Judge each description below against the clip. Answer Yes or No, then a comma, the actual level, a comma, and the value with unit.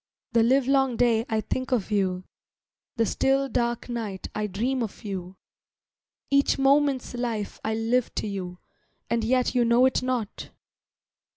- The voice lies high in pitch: Yes, high, 235 Hz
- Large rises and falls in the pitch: No, average, 3.3 semitones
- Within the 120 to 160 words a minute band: Yes, average, 150 wpm